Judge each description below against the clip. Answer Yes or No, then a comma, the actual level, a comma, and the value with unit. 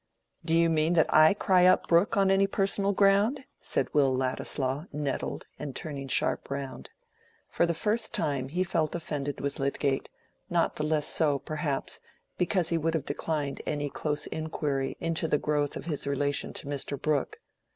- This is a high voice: No, medium, 155 Hz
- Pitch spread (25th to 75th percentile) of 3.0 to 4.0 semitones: Yes, average, 3.3 semitones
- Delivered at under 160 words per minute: No, average, 170 wpm